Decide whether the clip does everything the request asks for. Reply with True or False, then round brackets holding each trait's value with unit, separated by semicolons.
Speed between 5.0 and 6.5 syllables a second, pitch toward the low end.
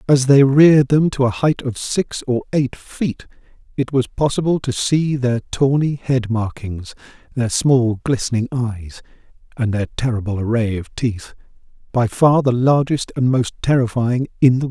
False (4.4 syllables/s; 125 Hz)